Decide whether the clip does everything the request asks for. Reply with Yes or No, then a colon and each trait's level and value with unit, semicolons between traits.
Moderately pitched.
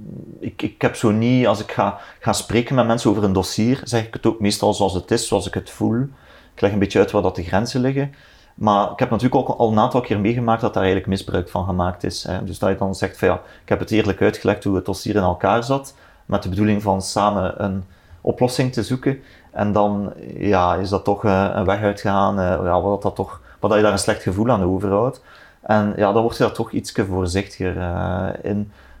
No: low, 100 Hz